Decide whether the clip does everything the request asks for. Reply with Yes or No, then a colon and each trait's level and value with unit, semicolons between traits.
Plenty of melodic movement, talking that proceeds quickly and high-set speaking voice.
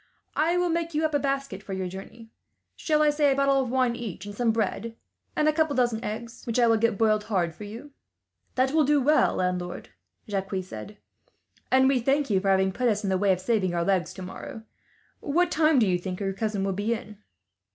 Yes: wide, 6.1 semitones; fast, 230 wpm; high, 225 Hz